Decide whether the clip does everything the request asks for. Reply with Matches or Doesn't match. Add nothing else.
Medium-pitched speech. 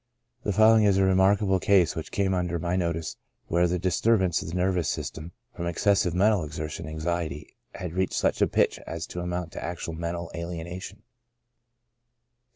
Doesn't match